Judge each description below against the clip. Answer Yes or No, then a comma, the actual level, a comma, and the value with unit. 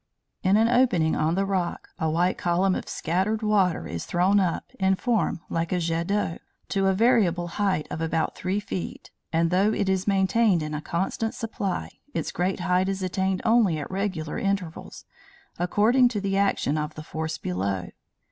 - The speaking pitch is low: No, medium, 185 Hz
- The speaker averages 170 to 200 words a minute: Yes, average, 180 wpm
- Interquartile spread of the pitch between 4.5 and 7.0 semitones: No, average, 3.3 semitones